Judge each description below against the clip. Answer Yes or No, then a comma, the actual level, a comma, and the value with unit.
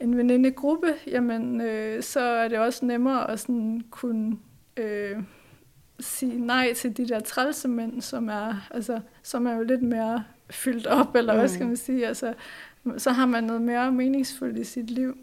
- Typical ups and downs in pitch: No, narrow, 2.0 semitones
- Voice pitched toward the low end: No, high, 240 Hz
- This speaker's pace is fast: No, average, 175 wpm